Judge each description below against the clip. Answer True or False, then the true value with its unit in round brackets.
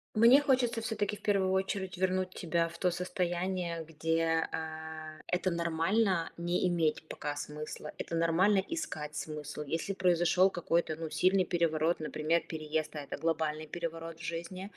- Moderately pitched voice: True (170 Hz)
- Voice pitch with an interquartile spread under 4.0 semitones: True (2.8 semitones)